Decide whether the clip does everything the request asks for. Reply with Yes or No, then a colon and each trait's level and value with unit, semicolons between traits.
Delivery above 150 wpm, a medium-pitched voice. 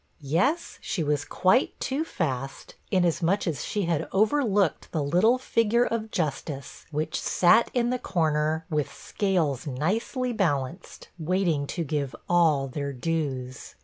No: slow, 135 wpm; medium, 165 Hz